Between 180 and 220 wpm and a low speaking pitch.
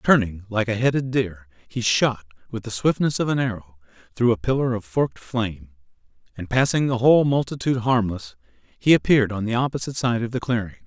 Yes: average, 190 wpm; low, 115 Hz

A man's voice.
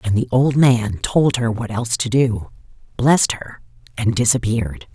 No: female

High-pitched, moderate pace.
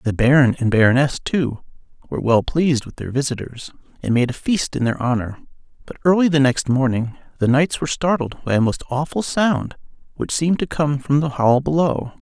No: low, 135 Hz; average, 195 wpm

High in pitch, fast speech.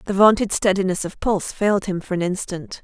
Yes: high, 195 Hz; fast, 210 wpm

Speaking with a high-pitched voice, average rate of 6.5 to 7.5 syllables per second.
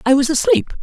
Yes: very high, 270 Hz; 7.0 syllables/s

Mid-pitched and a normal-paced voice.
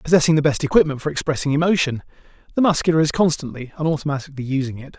Yes: medium, 150 Hz; average, 180 wpm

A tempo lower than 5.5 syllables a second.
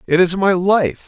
Yes: 4.3 syllables/s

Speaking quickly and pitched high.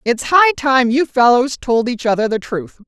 Yes: fast, 210 wpm; very high, 250 Hz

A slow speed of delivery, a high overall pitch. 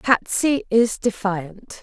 Yes: slow, 100 wpm; high, 215 Hz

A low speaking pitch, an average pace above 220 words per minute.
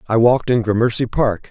No: low, 115 Hz; average, 200 wpm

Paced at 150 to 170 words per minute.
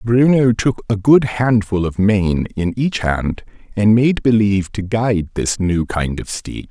No: average, 180 wpm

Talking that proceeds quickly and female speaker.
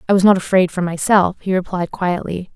Yes: fast, 210 wpm; female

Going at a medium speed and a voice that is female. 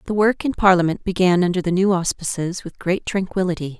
Yes: average, 190 wpm; female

